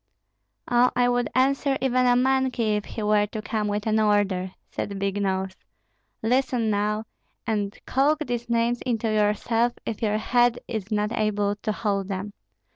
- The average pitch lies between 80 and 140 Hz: No, high, 220 Hz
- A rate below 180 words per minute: Yes, average, 165 wpm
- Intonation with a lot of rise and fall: No, average, 2.8 semitones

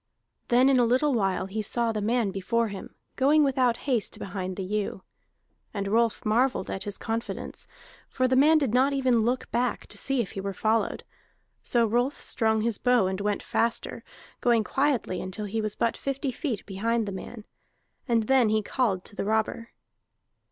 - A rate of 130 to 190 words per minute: Yes, average, 185 wpm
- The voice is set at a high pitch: Yes, high, 230 Hz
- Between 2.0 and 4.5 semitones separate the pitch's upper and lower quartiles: Yes, average, 3.4 semitones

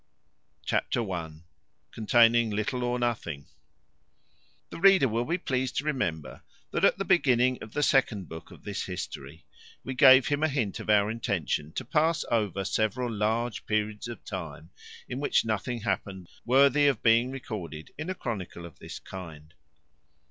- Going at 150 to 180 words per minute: Yes, average, 160 wpm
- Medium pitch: No, low, 115 Hz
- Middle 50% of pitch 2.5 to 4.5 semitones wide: No, average, 5.1 semitones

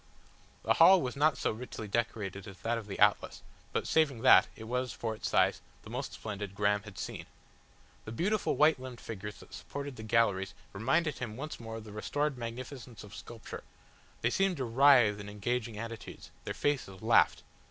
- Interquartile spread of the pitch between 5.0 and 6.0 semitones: No, average, 3.9 semitones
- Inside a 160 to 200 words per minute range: Yes, average, 185 wpm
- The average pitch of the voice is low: Yes, low, 115 Hz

